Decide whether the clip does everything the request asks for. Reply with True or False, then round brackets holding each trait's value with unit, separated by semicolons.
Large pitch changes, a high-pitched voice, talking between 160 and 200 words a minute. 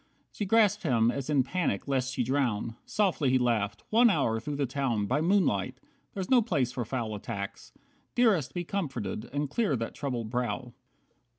False (7.0 semitones; 130 Hz; 175 wpm)